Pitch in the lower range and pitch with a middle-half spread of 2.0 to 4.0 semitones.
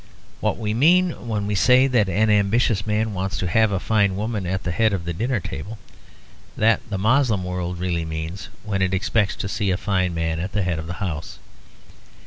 Yes: low, 100 Hz; average, 3.4 semitones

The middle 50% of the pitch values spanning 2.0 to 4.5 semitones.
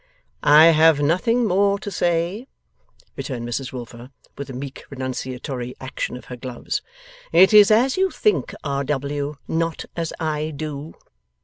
No: average, 5.0 semitones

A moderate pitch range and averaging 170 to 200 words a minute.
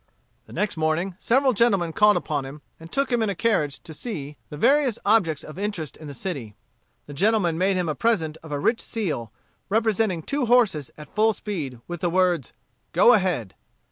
No: wide, 6.3 semitones; average, 195 wpm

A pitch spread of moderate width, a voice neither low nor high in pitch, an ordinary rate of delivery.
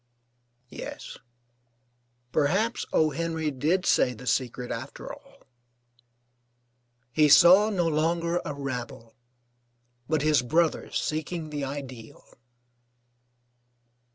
No: average, 4.0 semitones; medium, 155 Hz; slow, 95 wpm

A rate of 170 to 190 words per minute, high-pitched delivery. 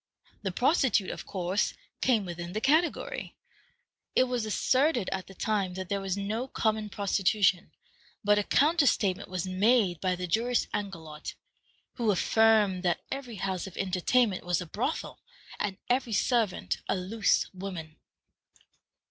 No: average, 145 wpm; high, 200 Hz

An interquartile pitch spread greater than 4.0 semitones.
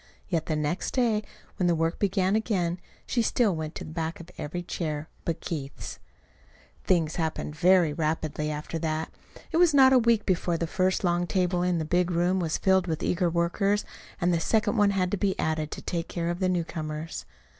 No: average, 2.9 semitones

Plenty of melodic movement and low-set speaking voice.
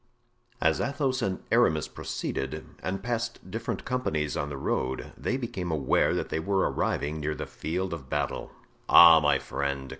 Yes: wide, 7.4 semitones; very low, 80 Hz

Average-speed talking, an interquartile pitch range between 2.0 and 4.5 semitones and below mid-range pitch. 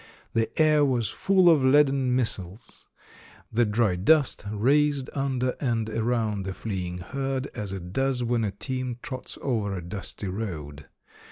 No: average, 150 wpm; average, 4.9 semitones; low, 120 Hz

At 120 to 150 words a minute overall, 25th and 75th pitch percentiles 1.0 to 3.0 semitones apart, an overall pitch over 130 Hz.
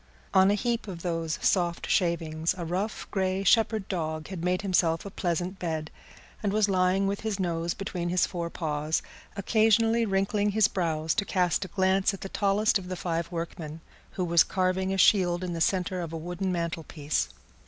No: average, 185 wpm; average, 2.7 semitones; medium, 185 Hz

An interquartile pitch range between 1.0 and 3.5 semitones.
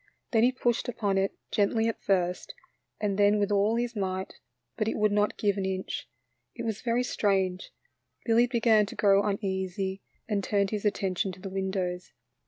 Yes: narrow, 2.5 semitones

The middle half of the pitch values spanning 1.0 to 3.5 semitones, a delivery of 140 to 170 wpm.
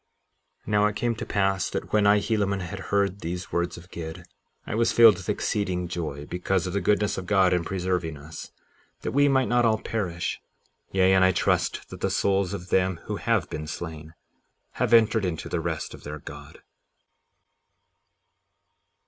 No: average, 3.0 semitones; average, 180 wpm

